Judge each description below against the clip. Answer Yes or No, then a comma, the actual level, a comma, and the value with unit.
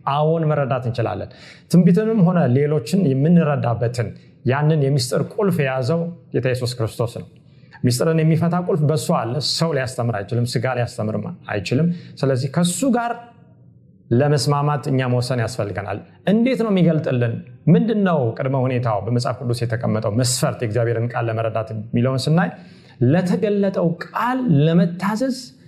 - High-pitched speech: No, medium, 140 Hz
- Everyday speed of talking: No, fast, 120 wpm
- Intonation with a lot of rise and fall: Yes, wide, 5.9 semitones